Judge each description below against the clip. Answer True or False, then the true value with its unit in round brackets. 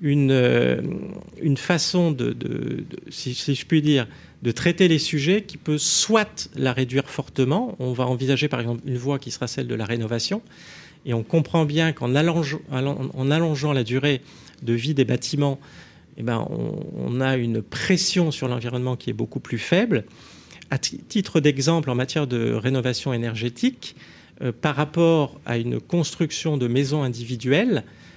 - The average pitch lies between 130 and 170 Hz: True (140 Hz)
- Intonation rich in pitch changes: False (4.3 semitones)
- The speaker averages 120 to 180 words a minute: True (170 wpm)